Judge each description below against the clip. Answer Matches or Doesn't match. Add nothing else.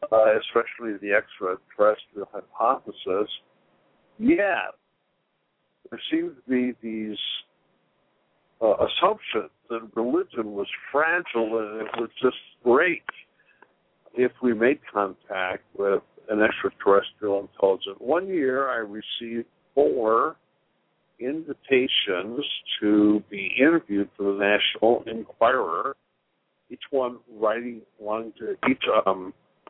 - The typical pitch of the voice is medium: Doesn't match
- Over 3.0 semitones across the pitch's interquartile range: Matches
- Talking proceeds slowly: Matches